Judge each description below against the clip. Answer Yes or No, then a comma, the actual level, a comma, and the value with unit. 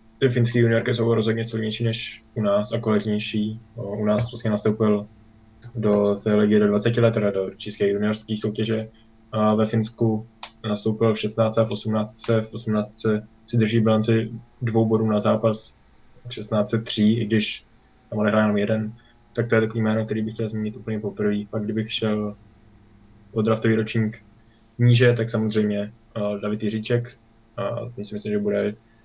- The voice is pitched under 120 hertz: Yes, low, 110 Hz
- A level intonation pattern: Yes, narrow, 1.2 semitones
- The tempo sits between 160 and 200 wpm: Yes, fast, 165 wpm